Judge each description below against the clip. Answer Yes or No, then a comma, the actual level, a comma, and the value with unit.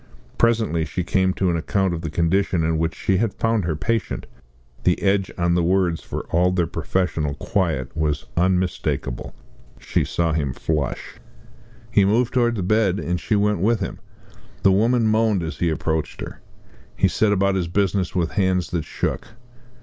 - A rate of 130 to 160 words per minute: No, average, 175 wpm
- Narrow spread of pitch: No, average, 3.6 semitones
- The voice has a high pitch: No, very low, 90 Hz